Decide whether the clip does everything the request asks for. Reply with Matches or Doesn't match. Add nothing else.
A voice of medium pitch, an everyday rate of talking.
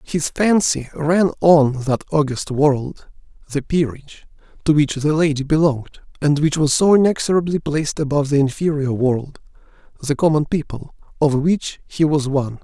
Matches